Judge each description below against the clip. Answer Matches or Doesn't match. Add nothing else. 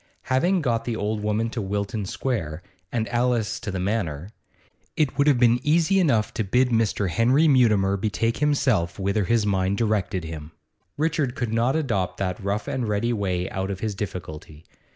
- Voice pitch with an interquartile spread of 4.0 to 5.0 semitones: Matches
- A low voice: Matches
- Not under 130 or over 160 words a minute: Doesn't match